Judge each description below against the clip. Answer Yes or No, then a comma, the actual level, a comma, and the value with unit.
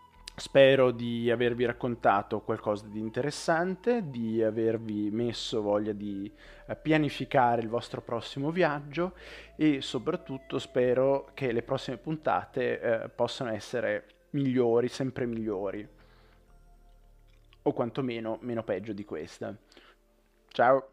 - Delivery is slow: Yes, slow, 105 wpm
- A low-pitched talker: Yes, low, 120 Hz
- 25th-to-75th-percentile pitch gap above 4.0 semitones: No, average, 3.7 semitones